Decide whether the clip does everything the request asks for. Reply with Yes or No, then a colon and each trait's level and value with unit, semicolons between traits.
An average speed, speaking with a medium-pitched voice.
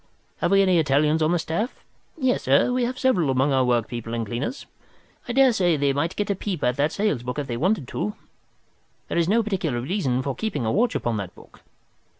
No: fast, 215 wpm; medium, 155 Hz